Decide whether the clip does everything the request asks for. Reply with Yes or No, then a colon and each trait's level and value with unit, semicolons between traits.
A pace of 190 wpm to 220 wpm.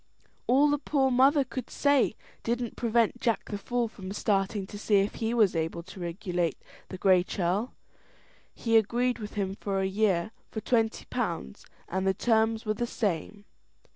No: average, 170 wpm